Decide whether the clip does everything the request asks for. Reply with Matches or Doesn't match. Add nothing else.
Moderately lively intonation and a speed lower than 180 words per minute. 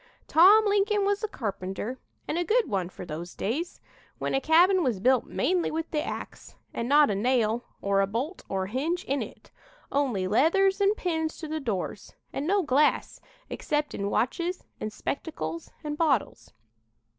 Doesn't match